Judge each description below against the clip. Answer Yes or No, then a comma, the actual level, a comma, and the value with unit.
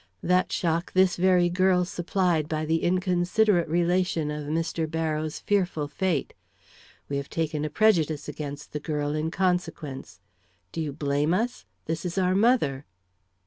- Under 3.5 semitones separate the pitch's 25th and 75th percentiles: Yes, average, 3.1 semitones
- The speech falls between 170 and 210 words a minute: No, average, 145 wpm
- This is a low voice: No, medium, 165 Hz